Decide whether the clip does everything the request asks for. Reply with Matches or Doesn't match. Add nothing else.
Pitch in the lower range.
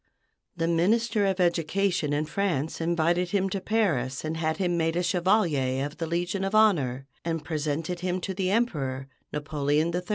Doesn't match